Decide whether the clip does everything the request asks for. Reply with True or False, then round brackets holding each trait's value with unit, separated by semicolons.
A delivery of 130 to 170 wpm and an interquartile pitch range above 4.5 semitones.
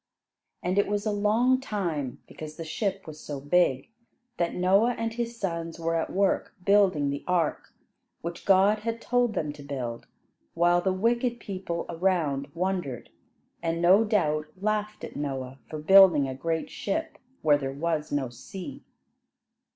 True (160 wpm; 5.4 semitones)